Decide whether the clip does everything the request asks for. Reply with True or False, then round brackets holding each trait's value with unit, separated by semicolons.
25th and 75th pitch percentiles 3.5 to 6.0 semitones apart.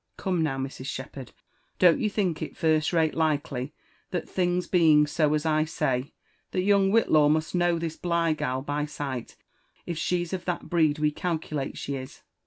False (3.1 semitones)